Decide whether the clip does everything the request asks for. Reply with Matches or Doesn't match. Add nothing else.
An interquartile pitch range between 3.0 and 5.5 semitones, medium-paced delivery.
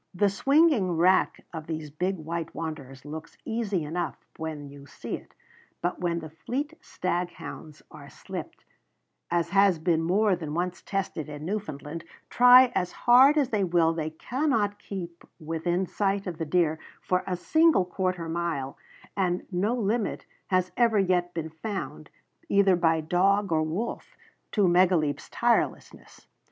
Matches